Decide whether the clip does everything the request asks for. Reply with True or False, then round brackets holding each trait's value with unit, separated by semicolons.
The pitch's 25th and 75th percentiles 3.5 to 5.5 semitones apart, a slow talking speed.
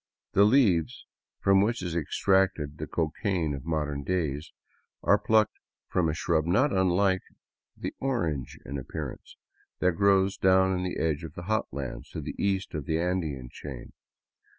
False (4.1 semitones; 170 wpm)